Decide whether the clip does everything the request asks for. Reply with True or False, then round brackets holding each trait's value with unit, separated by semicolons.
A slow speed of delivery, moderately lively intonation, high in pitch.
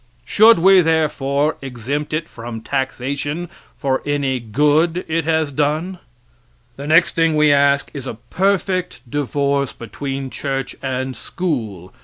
False (130 wpm; 3.3 semitones; 145 Hz)